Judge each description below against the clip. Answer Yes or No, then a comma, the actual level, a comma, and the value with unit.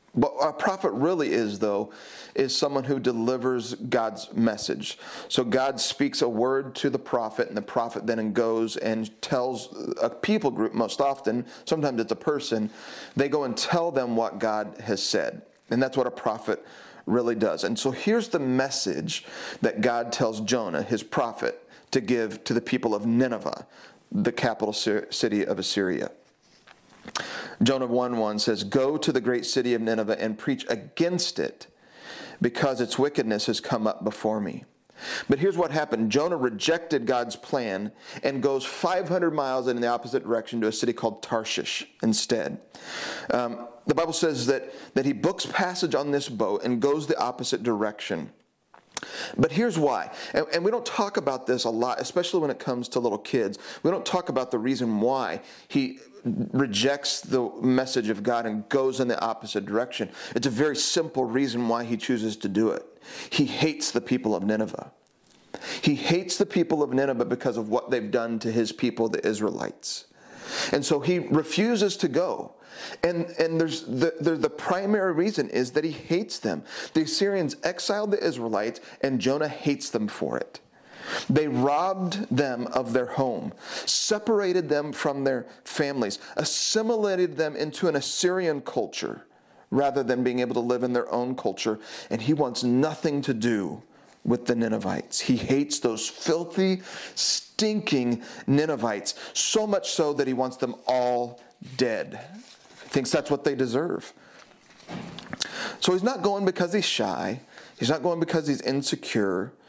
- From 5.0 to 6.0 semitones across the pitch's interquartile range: Yes, average, 5.3 semitones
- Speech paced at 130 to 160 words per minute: No, average, 170 wpm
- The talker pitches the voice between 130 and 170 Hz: Yes, low, 135 Hz